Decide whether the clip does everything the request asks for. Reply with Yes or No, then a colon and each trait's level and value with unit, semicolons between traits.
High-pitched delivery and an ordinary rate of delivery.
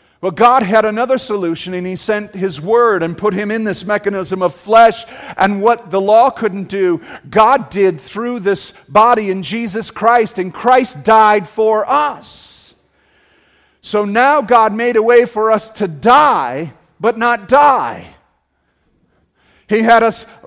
Yes: high, 215 Hz; average, 155 wpm